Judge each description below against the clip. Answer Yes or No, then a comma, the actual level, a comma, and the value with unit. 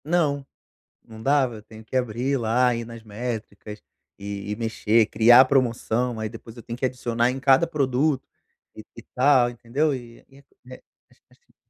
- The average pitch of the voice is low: Yes, low, 120 Hz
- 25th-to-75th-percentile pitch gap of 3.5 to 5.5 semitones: No, average, 2.9 semitones